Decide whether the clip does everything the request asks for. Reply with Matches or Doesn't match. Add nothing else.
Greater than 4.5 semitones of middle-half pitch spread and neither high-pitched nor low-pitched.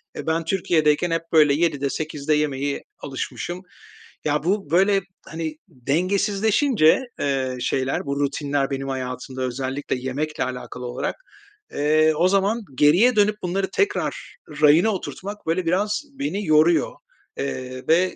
Matches